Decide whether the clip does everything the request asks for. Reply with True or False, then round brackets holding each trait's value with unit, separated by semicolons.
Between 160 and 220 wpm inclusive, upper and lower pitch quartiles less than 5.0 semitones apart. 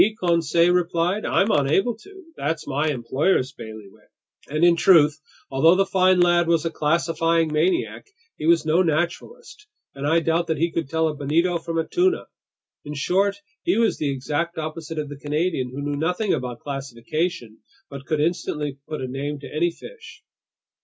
True (175 wpm; 3.3 semitones)